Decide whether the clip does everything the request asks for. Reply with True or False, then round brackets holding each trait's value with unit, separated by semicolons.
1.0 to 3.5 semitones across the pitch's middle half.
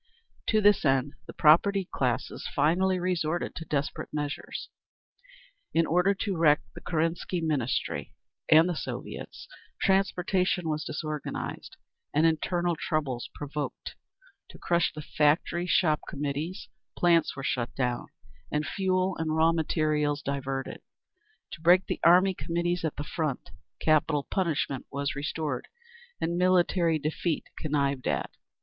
True (3.1 semitones)